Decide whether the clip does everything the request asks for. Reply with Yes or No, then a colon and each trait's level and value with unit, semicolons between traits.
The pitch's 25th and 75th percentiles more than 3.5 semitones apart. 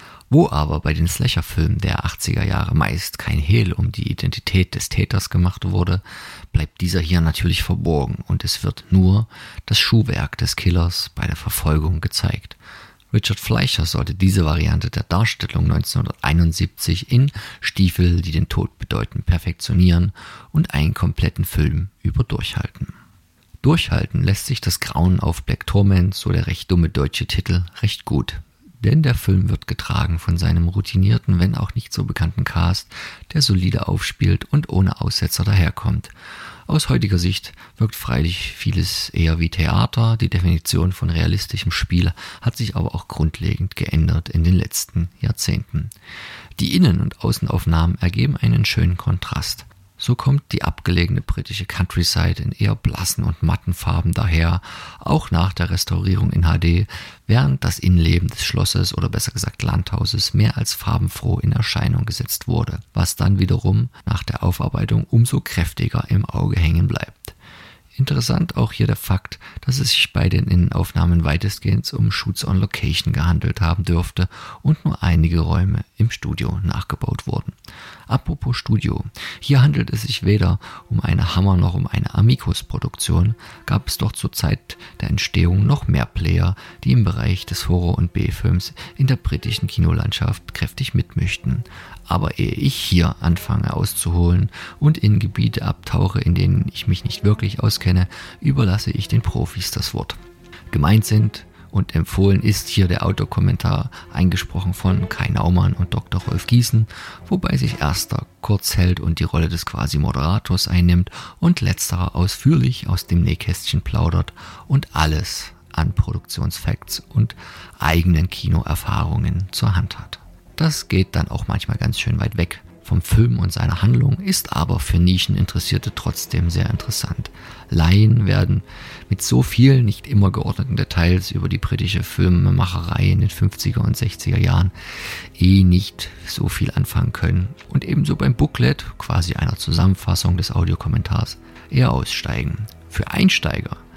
Yes: average, 4.5 semitones